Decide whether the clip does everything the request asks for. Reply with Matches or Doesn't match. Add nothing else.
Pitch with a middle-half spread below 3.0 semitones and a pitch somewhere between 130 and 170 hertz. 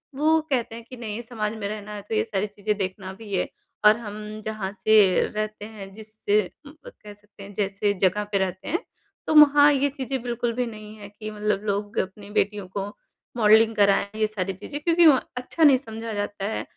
Doesn't match